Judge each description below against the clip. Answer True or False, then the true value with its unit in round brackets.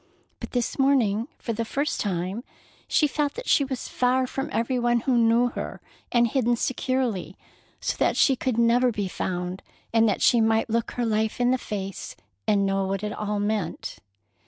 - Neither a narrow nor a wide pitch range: True (3.3 semitones)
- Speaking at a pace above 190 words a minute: False (185 wpm)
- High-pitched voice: True (230 Hz)